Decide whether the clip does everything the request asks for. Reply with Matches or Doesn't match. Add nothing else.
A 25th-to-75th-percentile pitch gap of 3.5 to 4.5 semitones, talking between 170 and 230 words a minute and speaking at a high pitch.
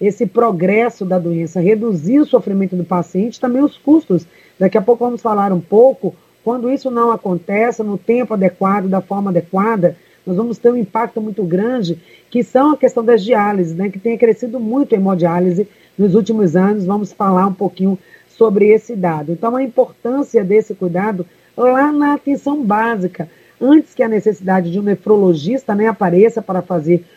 Matches